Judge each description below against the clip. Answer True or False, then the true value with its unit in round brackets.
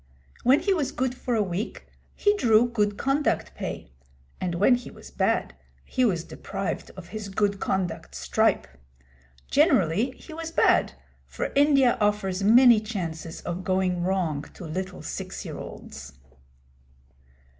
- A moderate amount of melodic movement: False (5.7 semitones)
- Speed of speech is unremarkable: True (145 wpm)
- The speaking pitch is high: True (210 Hz)